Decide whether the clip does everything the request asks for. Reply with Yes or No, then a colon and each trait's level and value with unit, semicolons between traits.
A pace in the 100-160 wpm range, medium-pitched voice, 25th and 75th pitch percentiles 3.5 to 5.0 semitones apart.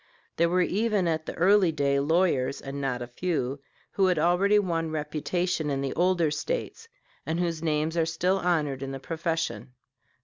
No: average, 175 wpm; medium, 165 Hz; average, 4.0 semitones